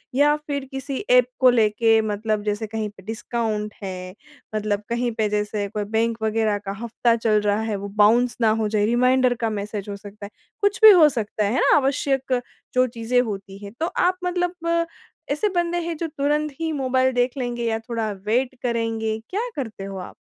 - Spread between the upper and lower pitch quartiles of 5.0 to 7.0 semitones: No, average, 3.8 semitones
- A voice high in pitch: Yes, high, 230 Hz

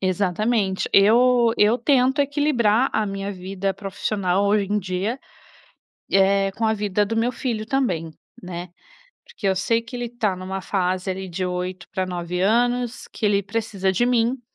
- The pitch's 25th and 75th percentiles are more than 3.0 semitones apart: Yes, average, 3.8 semitones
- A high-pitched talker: Yes, high, 200 Hz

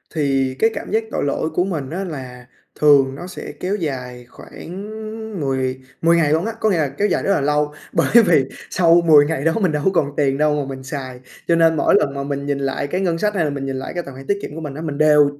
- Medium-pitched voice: Yes, medium, 150 Hz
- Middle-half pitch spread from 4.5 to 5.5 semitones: No, average, 3.5 semitones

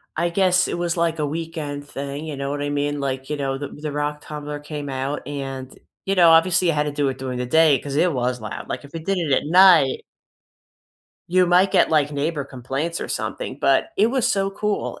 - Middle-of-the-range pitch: Yes, medium, 150 Hz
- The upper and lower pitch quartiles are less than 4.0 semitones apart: Yes, average, 3.4 semitones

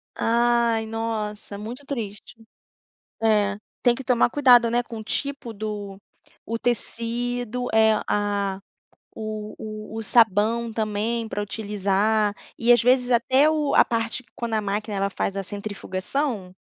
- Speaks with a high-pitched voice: Yes, high, 225 Hz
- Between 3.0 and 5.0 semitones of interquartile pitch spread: No, narrow, 2.5 semitones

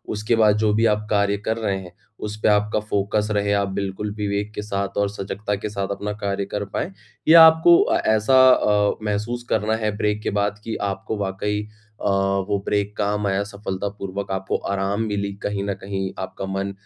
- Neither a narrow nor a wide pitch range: No, narrow, 1.1 semitones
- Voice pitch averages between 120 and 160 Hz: No, low, 105 Hz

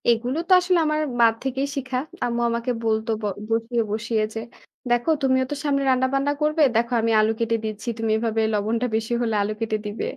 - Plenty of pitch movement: No, average, 2.8 semitones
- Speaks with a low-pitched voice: No, high, 235 Hz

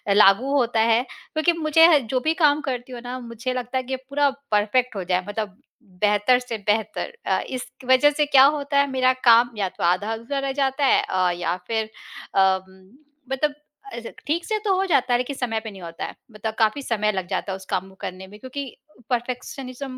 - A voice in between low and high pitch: No, high, 245 Hz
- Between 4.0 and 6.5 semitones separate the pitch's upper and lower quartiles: Yes, average, 4.5 semitones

